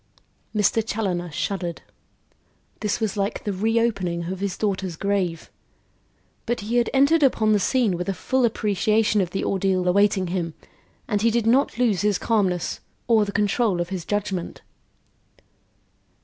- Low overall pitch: No, high, 205 Hz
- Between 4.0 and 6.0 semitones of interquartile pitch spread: No, average, 3.3 semitones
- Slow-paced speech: No, average, 150 wpm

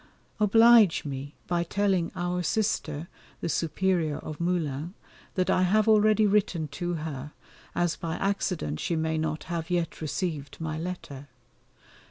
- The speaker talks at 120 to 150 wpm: Yes, average, 140 wpm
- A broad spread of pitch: No, average, 3.4 semitones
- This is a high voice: No, medium, 170 Hz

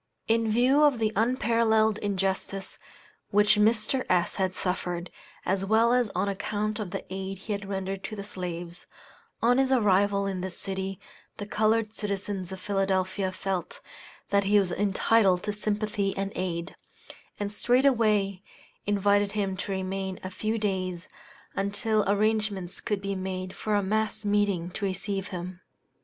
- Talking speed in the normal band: Yes, average, 150 wpm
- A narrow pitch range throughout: Yes, narrow, 2.1 semitones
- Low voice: No, high, 200 Hz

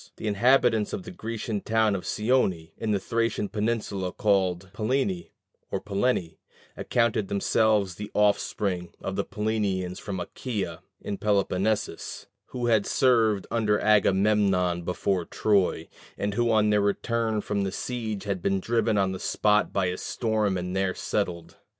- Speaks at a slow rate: No, average, 150 wpm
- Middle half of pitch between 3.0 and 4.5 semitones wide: No, narrow, 2.6 semitones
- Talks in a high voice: No, low, 105 Hz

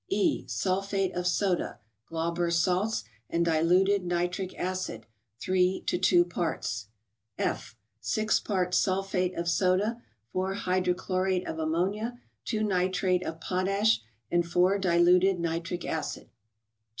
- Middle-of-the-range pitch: Yes, medium, 180 Hz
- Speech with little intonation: Yes, narrow, 2.0 semitones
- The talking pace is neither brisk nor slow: No, slow, 125 wpm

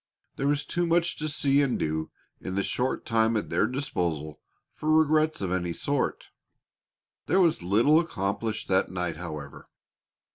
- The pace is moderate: Yes, average, 155 wpm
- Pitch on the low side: Yes, low, 115 Hz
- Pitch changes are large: Yes, wide, 9.0 semitones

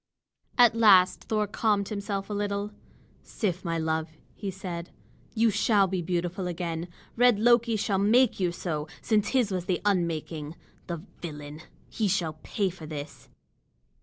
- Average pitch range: Yes, average, 3.7 semitones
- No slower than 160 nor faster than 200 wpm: No, average, 150 wpm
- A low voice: No, high, 190 Hz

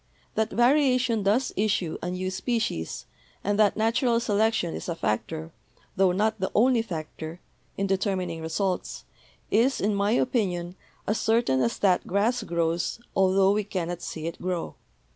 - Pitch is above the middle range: Yes, high, 195 Hz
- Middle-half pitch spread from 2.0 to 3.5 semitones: No, average, 4.1 semitones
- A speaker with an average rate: Yes, average, 150 wpm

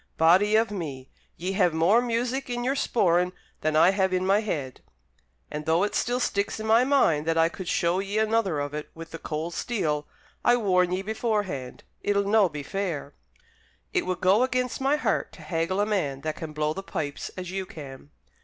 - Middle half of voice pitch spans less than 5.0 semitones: No, average, 5.3 semitones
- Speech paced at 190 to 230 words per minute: Yes, average, 200 wpm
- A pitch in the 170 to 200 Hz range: Yes, medium, 185 Hz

